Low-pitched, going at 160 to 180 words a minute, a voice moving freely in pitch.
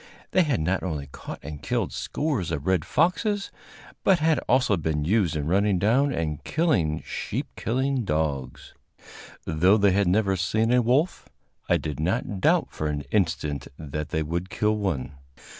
Yes: very low, 95 Hz; average, 165 wpm; wide, 7.3 semitones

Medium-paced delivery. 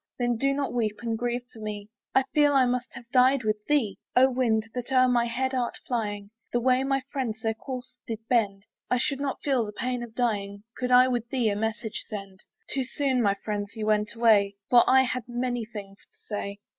No: fast, 220 wpm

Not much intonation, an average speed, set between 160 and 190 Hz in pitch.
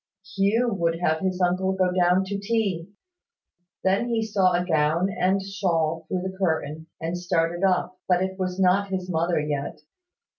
Yes: narrow, 2.3 semitones; average, 170 wpm; medium, 185 Hz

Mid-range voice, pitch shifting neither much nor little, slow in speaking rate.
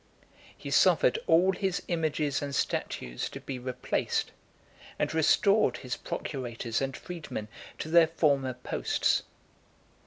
Yes: medium, 145 Hz; average, 4.8 semitones; slow, 120 wpm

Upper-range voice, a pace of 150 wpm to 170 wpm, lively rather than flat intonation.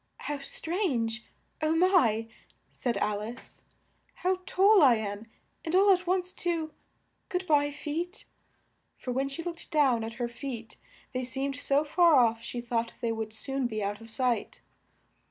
Yes: very high, 270 Hz; average, 160 wpm; wide, 6.5 semitones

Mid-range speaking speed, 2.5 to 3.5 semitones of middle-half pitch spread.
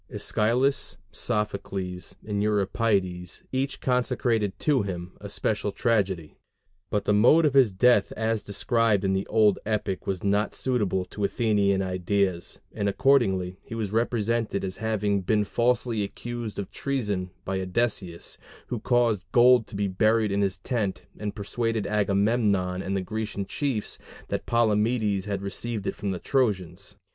Yes: average, 150 wpm; average, 3.0 semitones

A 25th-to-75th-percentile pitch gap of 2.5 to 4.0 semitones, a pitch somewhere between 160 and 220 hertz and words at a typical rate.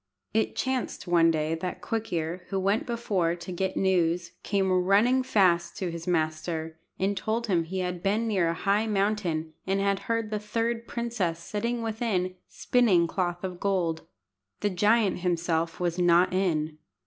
Yes: average, 3.7 semitones; medium, 185 Hz; average, 165 wpm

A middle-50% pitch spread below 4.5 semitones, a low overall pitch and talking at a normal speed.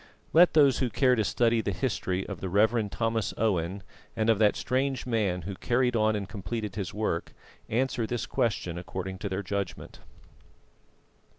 Yes: average, 3.8 semitones; low, 110 Hz; average, 170 wpm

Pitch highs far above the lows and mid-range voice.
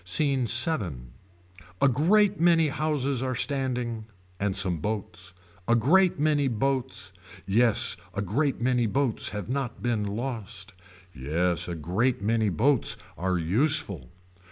No: wide, 5.9 semitones; low, 120 Hz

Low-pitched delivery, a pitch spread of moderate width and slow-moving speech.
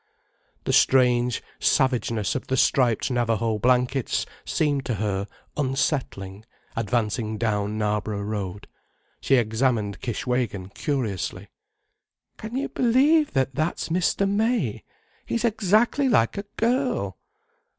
No: low, 125 Hz; wide, 7.5 semitones; slow, 105 wpm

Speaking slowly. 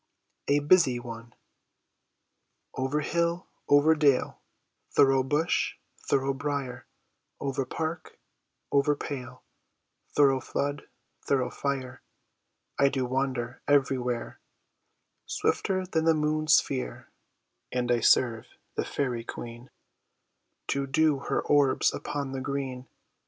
Yes: slow, 105 wpm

